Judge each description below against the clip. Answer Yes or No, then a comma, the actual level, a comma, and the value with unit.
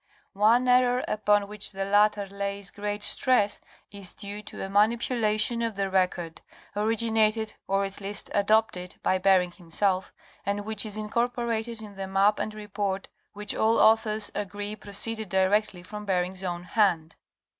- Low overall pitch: No, high, 205 Hz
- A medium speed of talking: Yes, average, 155 wpm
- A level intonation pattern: Yes, narrow, 2.0 semitones